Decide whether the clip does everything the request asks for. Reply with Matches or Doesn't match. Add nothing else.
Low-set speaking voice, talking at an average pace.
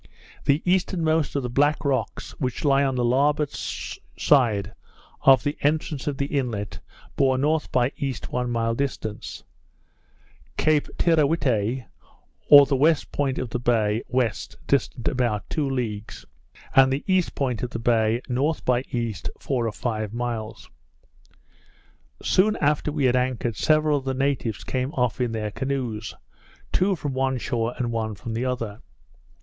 Matches